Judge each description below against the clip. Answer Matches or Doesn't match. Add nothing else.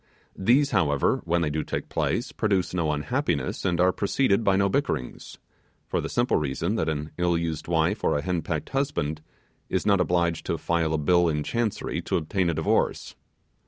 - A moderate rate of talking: Matches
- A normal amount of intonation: Matches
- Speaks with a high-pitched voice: Doesn't match